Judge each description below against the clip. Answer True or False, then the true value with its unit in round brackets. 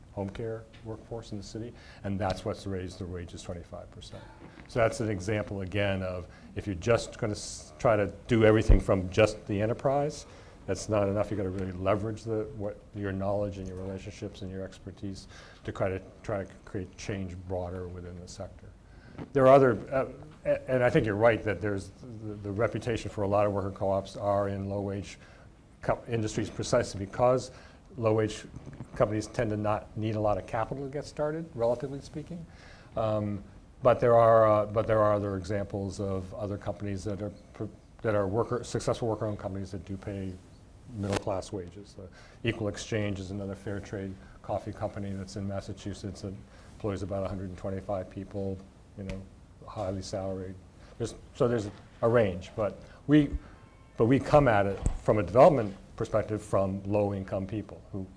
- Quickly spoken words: False (180 wpm)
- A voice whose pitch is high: False (100 Hz)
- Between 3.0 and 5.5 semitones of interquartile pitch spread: False (2.4 semitones)